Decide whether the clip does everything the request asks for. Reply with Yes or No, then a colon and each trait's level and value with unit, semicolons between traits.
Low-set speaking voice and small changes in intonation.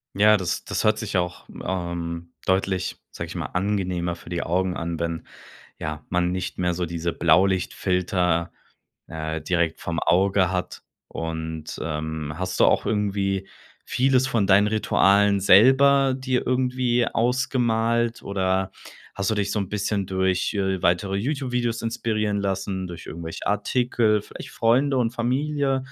No: very low, 95 Hz; average, 4.6 semitones